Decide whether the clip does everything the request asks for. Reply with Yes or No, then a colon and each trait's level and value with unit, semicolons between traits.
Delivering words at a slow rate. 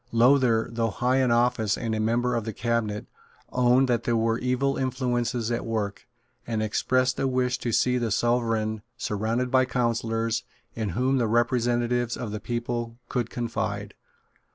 No: average, 160 wpm